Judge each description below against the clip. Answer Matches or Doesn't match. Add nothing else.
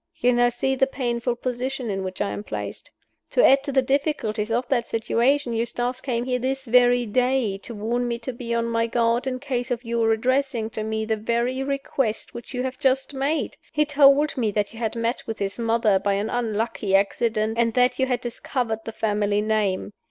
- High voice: Matches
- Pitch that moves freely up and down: Doesn't match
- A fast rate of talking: Matches